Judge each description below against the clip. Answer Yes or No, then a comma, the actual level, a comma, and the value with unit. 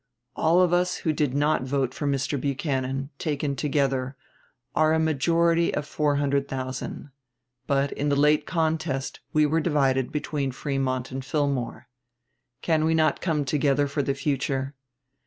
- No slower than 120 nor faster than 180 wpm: Yes, average, 155 wpm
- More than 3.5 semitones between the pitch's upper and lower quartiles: No, narrow, 2.4 semitones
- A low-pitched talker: No, medium, 145 Hz